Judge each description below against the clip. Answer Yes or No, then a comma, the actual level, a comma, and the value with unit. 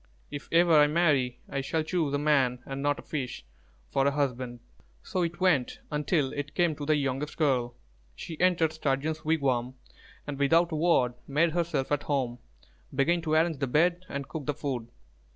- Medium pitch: Yes, medium, 145 Hz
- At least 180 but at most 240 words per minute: Yes, average, 185 wpm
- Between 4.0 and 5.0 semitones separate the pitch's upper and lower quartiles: No, average, 3.1 semitones